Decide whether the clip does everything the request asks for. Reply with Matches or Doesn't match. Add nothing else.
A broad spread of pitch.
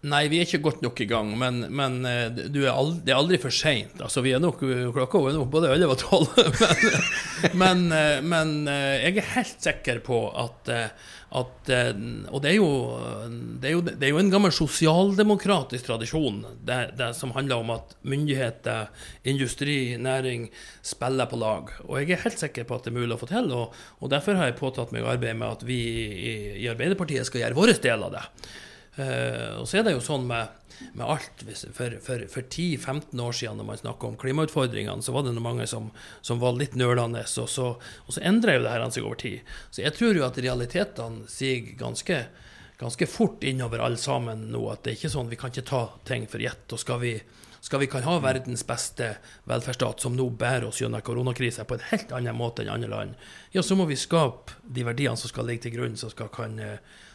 Doesn't match